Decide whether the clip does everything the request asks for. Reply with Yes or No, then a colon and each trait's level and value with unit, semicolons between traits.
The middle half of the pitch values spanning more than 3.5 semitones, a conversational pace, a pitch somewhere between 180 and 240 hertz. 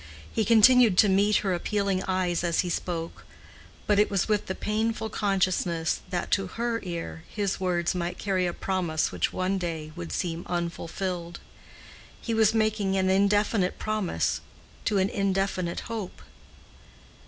No: average, 3.1 semitones; average, 150 wpm; high, 190 Hz